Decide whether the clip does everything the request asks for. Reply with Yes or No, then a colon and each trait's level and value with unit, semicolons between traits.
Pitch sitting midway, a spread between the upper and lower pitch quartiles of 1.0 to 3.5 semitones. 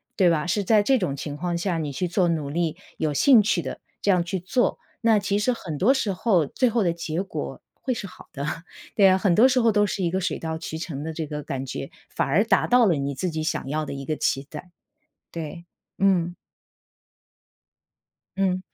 No: medium, 175 Hz; average, 4.5 semitones